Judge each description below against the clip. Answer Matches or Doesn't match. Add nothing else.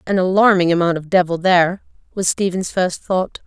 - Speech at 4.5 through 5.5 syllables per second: Matches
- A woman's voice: Matches